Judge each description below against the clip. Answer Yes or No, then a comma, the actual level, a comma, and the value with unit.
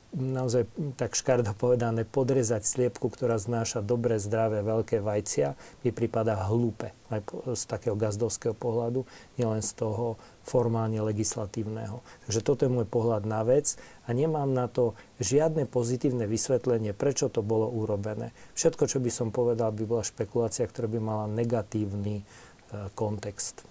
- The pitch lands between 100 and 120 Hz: Yes, low, 115 Hz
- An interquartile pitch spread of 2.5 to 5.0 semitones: No, narrow, 2.1 semitones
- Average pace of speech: Yes, average, 140 wpm